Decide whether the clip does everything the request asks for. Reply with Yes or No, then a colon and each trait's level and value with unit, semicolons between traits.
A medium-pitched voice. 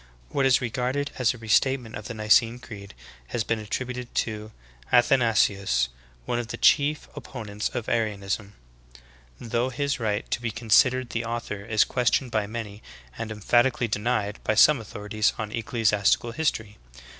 No: low, 115 Hz